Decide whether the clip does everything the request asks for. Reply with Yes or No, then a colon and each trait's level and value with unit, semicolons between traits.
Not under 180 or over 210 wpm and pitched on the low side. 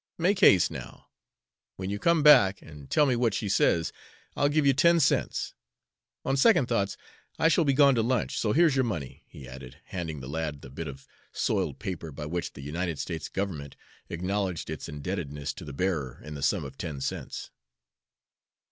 Yes: average, 190 wpm; very low, 90 Hz